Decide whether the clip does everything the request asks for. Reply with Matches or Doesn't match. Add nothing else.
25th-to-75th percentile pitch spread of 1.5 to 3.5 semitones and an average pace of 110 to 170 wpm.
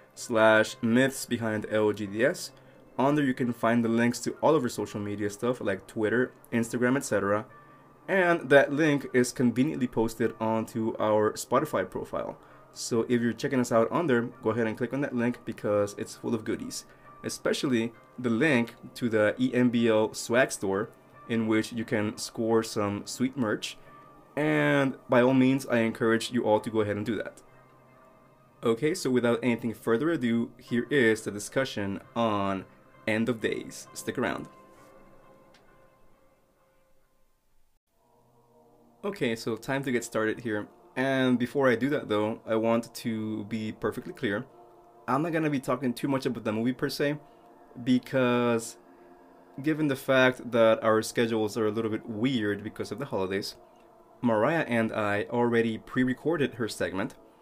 Matches